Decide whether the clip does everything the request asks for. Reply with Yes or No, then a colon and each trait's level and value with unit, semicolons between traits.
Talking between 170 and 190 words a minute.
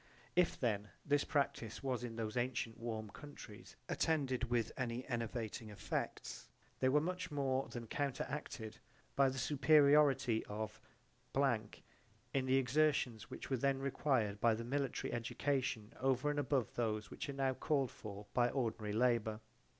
No: average, 150 wpm